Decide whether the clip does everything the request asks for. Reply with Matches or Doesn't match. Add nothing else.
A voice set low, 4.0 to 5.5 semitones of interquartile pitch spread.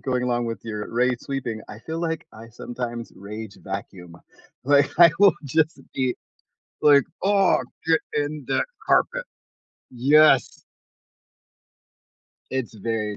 Matches